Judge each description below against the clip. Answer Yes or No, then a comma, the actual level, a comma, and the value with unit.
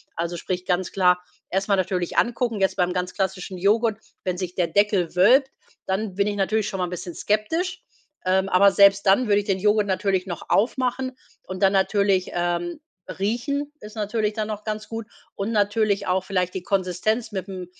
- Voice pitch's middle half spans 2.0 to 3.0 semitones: Yes, narrow, 2.6 semitones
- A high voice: Yes, high, 195 Hz